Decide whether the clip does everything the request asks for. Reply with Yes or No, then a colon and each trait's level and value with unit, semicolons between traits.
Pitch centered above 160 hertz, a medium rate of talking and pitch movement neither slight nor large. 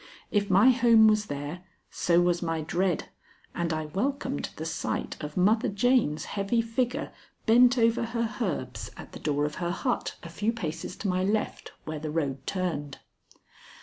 No: high, 190 Hz; average, 170 wpm; wide, 6.0 semitones